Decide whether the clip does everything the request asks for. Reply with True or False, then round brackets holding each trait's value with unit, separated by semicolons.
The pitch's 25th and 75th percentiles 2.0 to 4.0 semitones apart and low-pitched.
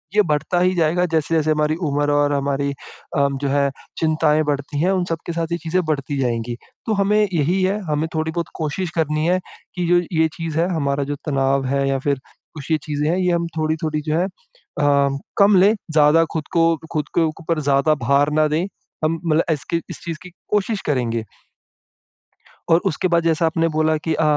False (2.8 semitones; 155 Hz)